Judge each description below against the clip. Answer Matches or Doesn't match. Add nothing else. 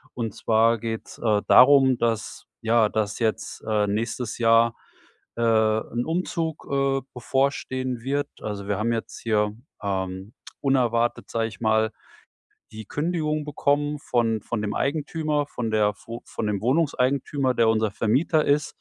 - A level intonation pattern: Doesn't match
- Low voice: Matches